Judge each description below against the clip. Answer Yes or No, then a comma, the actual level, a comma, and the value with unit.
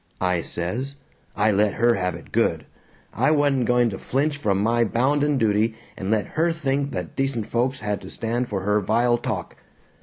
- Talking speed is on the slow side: No, average, 185 wpm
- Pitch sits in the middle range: No, low, 120 Hz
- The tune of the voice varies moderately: Yes, average, 4.6 semitones